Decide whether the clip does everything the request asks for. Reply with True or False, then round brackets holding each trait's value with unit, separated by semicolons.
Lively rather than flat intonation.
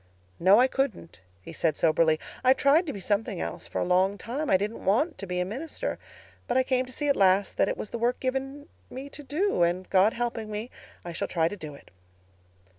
True (6.3 semitones)